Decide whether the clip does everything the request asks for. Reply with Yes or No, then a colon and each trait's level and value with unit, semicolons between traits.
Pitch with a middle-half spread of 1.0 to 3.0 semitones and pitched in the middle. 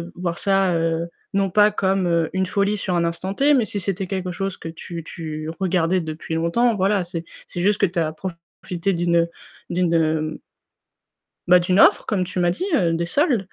Yes: narrow, 2.5 semitones; medium, 180 Hz